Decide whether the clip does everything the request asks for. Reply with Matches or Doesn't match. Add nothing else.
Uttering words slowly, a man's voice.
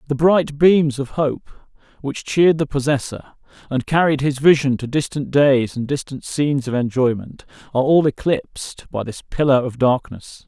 Doesn't match